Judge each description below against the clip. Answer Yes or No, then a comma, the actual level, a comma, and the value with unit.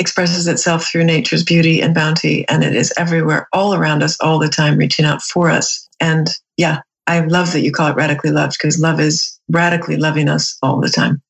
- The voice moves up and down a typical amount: No, narrow, 1.7 semitones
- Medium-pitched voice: Yes, medium, 160 Hz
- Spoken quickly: Yes, fast, 210 wpm